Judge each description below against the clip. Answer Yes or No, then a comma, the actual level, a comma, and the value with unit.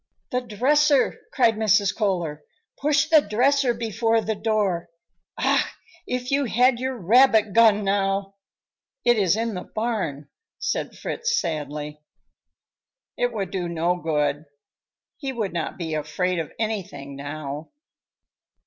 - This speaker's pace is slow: Yes, slow, 130 wpm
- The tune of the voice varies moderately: No, wide, 6.1 semitones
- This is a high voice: Yes, high, 210 Hz